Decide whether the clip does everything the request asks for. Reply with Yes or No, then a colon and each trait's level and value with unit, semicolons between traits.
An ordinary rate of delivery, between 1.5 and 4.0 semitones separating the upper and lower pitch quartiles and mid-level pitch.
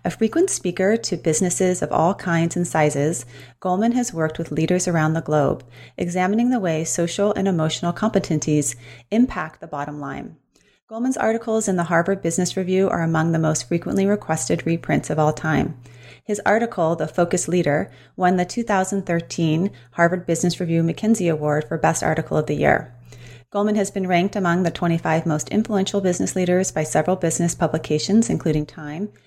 Yes: average, 170 wpm; average, 3.6 semitones; medium, 170 Hz